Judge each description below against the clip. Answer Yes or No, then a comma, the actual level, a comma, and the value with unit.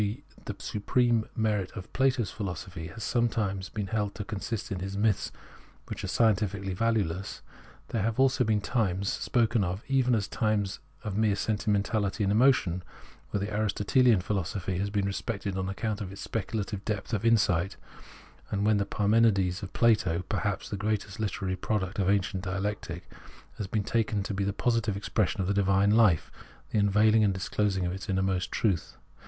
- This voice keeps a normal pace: Yes, average, 180 wpm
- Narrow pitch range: Yes, narrow, 2.3 semitones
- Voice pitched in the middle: No, low, 100 Hz